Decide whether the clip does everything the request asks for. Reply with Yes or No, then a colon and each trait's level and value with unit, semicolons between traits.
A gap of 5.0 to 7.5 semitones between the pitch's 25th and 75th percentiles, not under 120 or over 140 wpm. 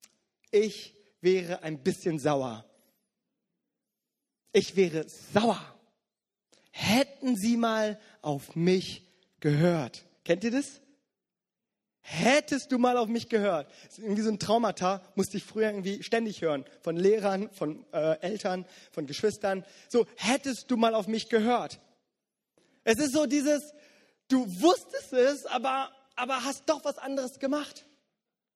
Yes: wide, 5.5 semitones; average, 130 wpm